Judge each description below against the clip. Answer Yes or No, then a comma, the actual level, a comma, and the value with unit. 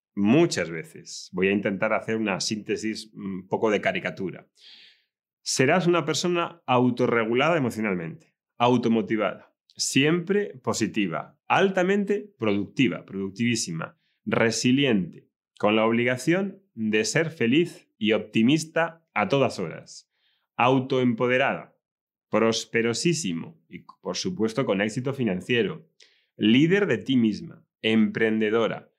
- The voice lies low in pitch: Yes, low, 120 Hz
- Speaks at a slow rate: Yes, slow, 100 wpm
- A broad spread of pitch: Yes, wide, 6.4 semitones